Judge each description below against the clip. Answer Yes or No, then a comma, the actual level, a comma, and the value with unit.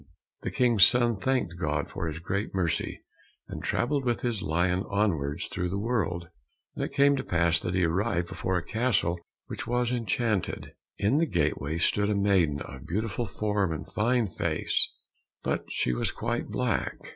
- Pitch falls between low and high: No, low, 100 Hz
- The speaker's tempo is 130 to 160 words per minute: No, average, 170 wpm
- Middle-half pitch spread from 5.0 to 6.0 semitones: Yes, wide, 5.5 semitones